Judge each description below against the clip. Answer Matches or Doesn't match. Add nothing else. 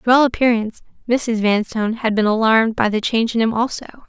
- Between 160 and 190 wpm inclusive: Doesn't match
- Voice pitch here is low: Doesn't match